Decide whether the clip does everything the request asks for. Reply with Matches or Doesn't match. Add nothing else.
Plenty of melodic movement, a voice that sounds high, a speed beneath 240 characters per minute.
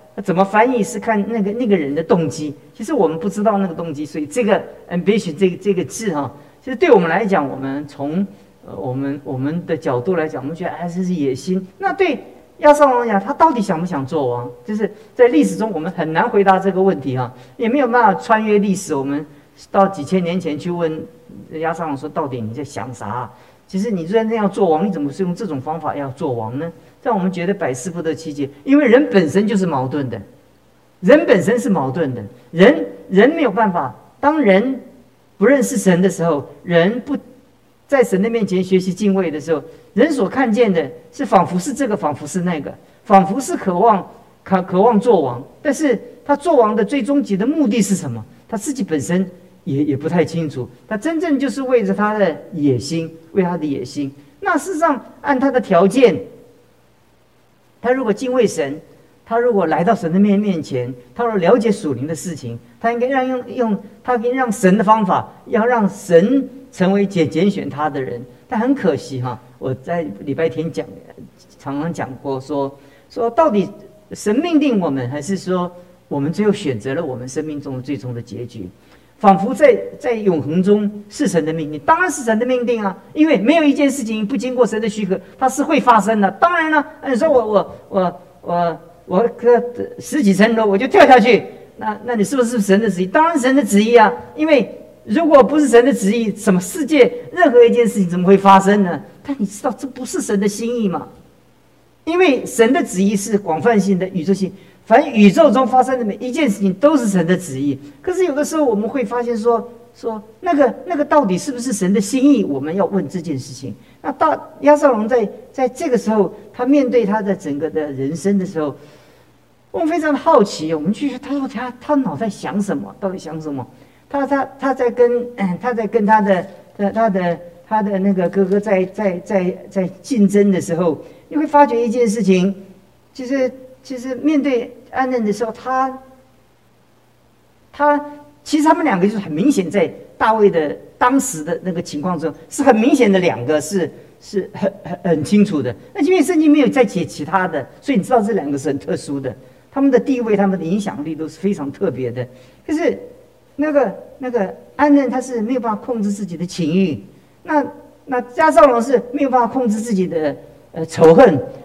Doesn't match